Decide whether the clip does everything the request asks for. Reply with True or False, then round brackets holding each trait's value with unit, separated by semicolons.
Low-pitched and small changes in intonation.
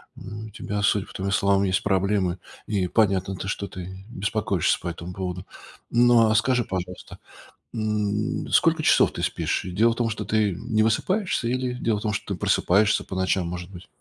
False (100 Hz; 3.0 semitones)